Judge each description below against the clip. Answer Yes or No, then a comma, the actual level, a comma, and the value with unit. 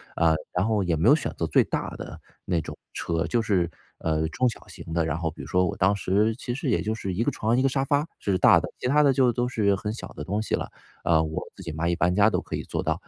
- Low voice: Yes, low, 100 Hz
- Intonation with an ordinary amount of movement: No, wide, 5.9 semitones